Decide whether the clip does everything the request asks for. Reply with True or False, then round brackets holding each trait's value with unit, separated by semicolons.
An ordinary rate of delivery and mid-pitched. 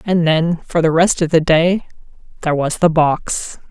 True (195 wpm; 165 Hz)